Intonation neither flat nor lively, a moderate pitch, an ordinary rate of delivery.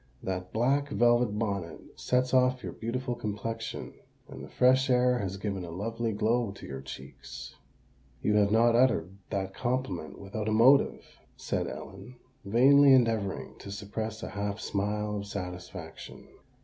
No: average, 3.8 semitones; low, 110 Hz; average, 150 wpm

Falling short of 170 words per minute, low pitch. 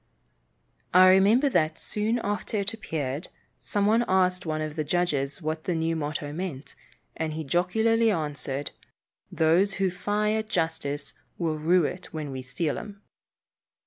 No: average, 150 wpm; medium, 170 Hz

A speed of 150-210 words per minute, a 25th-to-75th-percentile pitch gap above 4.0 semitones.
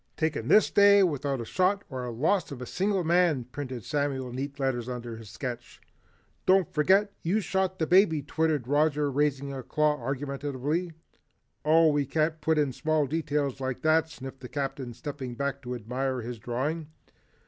No: average, 175 wpm; average, 3.7 semitones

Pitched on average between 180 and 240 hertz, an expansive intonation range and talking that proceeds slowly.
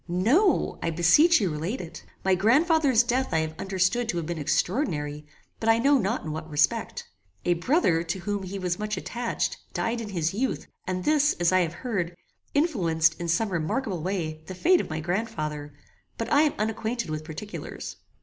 No: high, 190 Hz; wide, 6.1 semitones; average, 190 wpm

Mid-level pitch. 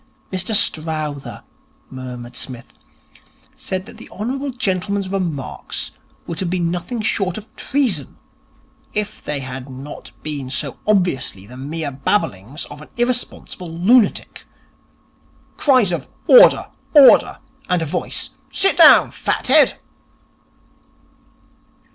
Yes: medium, 175 Hz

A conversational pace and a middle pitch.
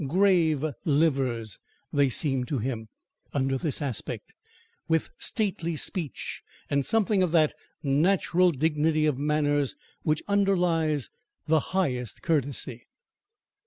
No: slow, 110 wpm; medium, 150 Hz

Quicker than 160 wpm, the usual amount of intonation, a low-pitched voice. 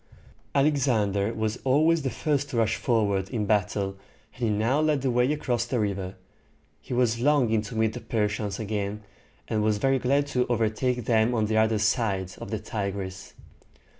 Yes: average, 175 wpm; average, 3.3 semitones; low, 110 Hz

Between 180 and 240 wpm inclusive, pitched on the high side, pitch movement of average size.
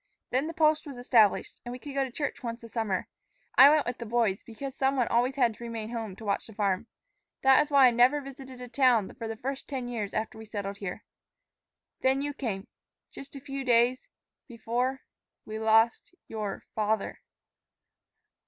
Yes: average, 190 wpm; high, 240 Hz; average, 3.4 semitones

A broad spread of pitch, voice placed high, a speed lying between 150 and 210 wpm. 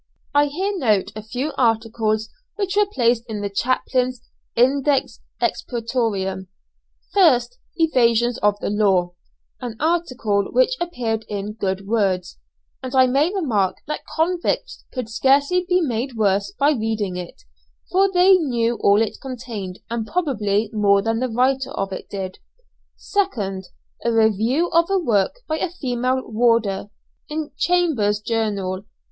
No: wide, 5.9 semitones; high, 235 Hz; average, 140 wpm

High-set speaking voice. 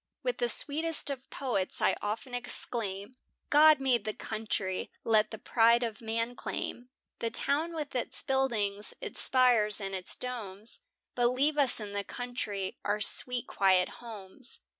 Yes: high, 235 Hz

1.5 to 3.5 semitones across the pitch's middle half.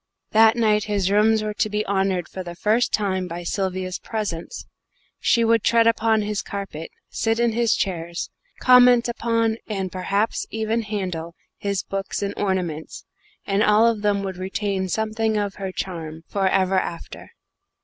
Yes: average, 2.8 semitones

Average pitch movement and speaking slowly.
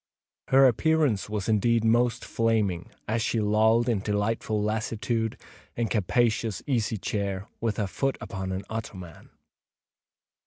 No: narrow, 2.2 semitones; slow, 130 wpm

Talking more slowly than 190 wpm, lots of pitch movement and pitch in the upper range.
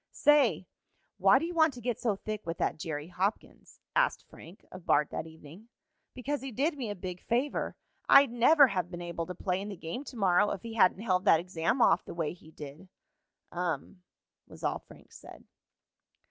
No: average, 200 wpm; wide, 6.1 semitones; high, 195 Hz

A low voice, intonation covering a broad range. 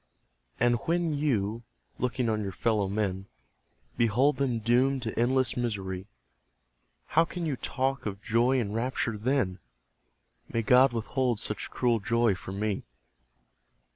No: low, 120 Hz; average, 3.7 semitones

